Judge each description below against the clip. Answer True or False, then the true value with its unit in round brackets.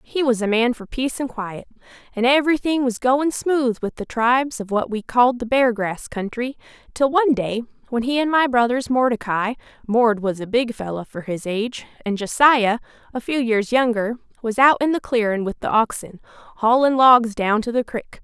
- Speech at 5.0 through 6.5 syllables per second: True (5.1 syllables/s)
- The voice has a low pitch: False (240 Hz)